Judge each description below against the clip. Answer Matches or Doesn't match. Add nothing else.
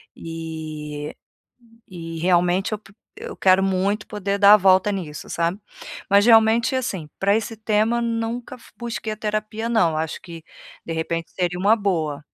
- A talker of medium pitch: Doesn't match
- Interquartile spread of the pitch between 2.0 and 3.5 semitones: Doesn't match